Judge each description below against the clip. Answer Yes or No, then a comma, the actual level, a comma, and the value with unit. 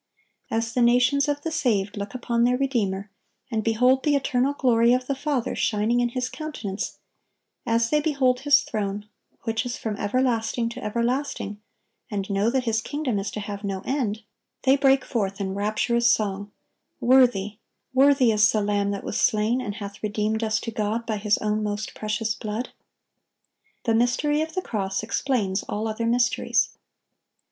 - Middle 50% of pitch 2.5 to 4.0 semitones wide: Yes, average, 3.4 semitones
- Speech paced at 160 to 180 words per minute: Yes, average, 170 wpm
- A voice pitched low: No, high, 230 Hz